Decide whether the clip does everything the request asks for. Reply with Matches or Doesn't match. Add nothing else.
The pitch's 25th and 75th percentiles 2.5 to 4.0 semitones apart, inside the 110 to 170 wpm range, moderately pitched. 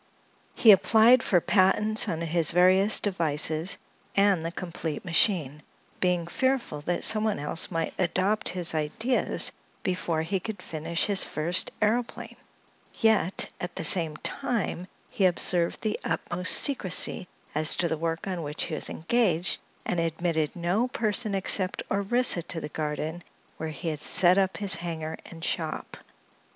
Matches